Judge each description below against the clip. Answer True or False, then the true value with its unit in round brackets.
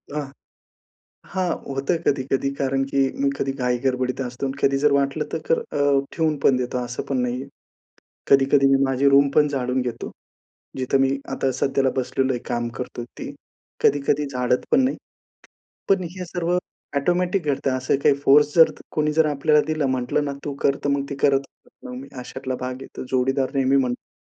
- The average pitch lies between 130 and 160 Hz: True (135 Hz)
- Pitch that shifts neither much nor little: False (2.2 semitones)